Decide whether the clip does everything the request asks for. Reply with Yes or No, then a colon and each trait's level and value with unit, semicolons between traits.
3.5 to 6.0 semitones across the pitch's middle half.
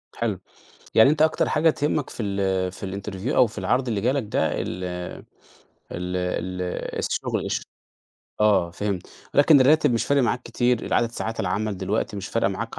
Yes: average, 5.0 semitones